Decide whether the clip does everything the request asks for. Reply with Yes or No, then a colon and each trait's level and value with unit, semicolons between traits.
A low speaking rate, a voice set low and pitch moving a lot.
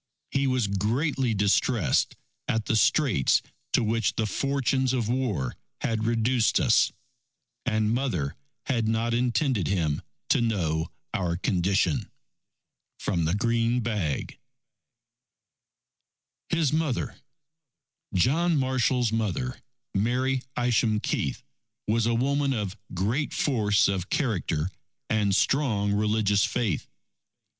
No: slow, 110 wpm; low, 115 Hz; average, 4.3 semitones